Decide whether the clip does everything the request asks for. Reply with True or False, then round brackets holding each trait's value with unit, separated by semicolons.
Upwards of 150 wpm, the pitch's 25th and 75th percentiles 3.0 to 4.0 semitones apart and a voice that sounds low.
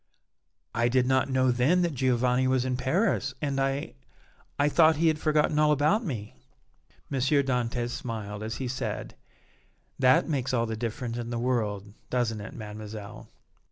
True (160 wpm; 3.3 semitones; 125 Hz)